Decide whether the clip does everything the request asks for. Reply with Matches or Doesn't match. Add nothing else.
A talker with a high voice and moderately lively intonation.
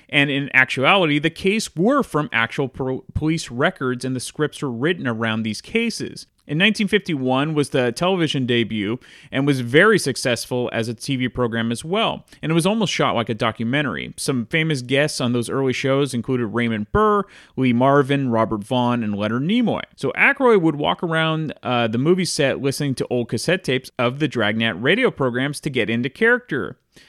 Doesn't match